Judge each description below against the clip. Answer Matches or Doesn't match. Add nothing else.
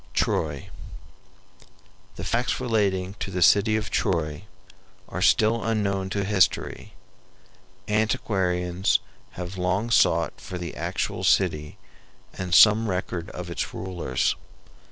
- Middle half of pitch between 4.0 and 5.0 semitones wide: Doesn't match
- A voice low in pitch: Matches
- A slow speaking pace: Matches